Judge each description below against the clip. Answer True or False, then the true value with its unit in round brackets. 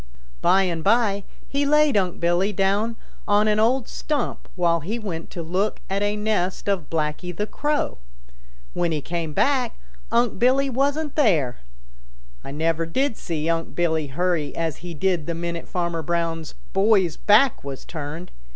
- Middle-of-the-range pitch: True (180 Hz)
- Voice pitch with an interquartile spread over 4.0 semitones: True (4.9 semitones)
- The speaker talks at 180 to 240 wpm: False (160 wpm)